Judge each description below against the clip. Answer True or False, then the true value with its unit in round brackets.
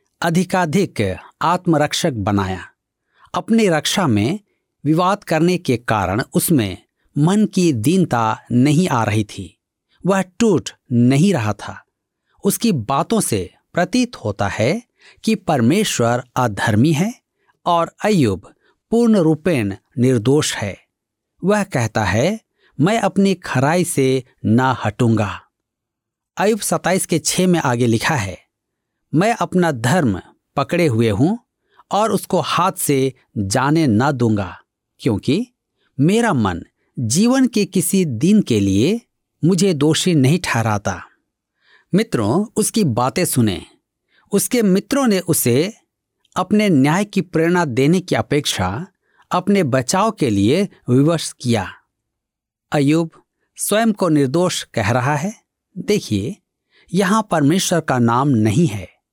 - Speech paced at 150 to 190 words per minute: False (120 wpm)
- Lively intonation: True (8.2 semitones)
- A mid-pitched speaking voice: True (155 Hz)